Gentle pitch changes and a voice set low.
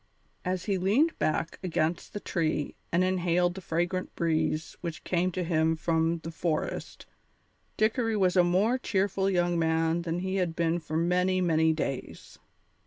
No: narrow, 2.3 semitones; medium, 175 Hz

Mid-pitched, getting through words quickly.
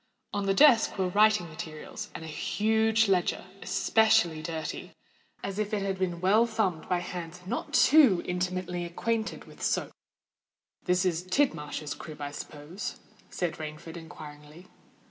No: medium, 180 Hz; average, 145 wpm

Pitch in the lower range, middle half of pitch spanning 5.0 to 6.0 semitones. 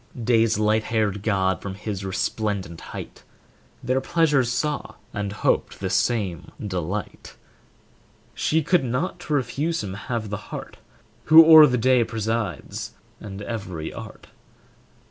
No: low, 110 Hz; average, 4.4 semitones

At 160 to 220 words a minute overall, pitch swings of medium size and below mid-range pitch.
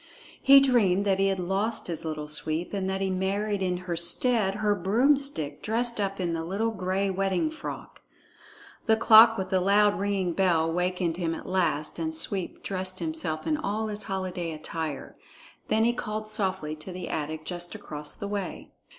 No: average, 180 wpm; average, 3.5 semitones; high, 190 Hz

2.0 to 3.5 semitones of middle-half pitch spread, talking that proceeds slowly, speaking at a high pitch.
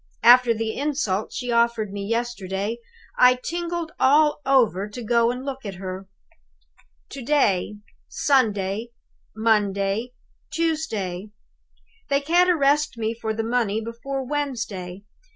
No: average, 4.9 semitones; slow, 120 wpm; high, 235 Hz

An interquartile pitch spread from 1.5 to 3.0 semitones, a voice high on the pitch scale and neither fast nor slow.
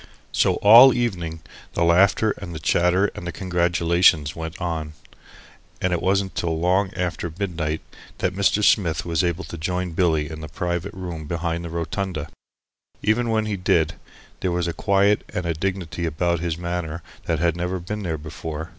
No: narrow, 2.5 semitones; very low, 85 Hz; average, 175 wpm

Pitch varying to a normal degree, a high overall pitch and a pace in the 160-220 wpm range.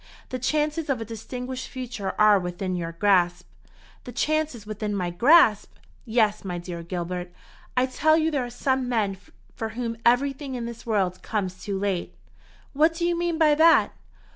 No: wide, 6.0 semitones; high, 230 Hz; average, 170 wpm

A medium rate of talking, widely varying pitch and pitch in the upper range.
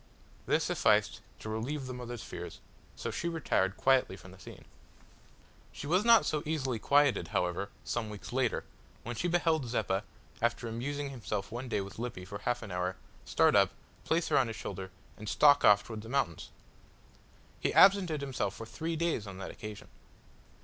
No: average, 175 wpm; wide, 5.9 semitones; low, 120 Hz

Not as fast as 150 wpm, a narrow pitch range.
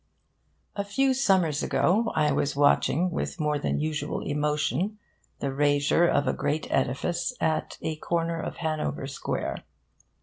No: average, 140 wpm; average, 3.1 semitones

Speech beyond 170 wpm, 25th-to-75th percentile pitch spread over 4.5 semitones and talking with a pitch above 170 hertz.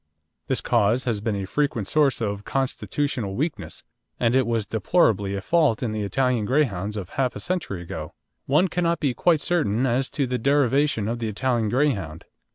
No: average, 180 wpm; wide, 5.5 semitones; low, 120 Hz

